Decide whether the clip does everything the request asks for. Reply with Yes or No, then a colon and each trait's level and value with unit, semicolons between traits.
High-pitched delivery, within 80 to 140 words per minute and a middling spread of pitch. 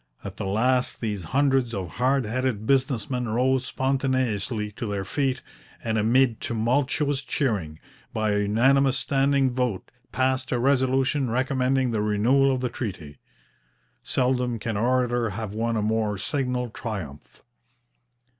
No: low, 125 Hz; slow, 135 wpm; average, 3.5 semitones